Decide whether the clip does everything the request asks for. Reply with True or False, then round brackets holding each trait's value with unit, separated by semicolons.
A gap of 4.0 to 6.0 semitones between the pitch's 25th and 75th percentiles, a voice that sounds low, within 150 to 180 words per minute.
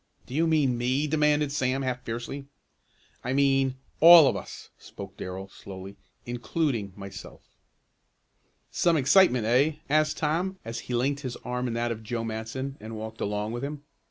True (4.4 semitones; 130 Hz; 160 wpm)